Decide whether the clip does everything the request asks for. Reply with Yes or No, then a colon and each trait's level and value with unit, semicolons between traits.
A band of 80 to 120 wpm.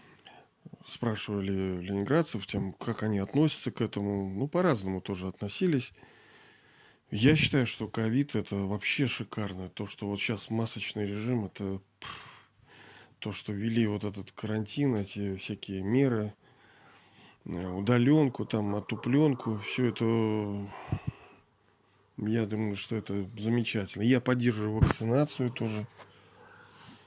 Yes: slow, 110 wpm